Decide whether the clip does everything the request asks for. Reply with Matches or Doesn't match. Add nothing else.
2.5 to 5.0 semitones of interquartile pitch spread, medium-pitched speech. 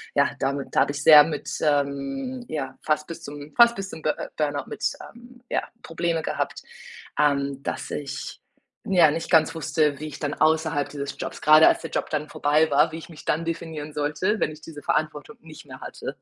Doesn't match